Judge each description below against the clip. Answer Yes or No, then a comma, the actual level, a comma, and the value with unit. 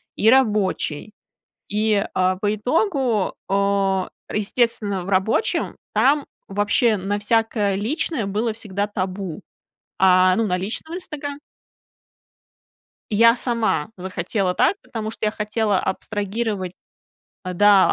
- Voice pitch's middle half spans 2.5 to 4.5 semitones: Yes, average, 3.0 semitones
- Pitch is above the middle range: Yes, high, 205 Hz